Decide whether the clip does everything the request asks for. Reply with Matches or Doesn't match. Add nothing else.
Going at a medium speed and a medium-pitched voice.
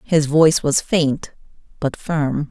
Matches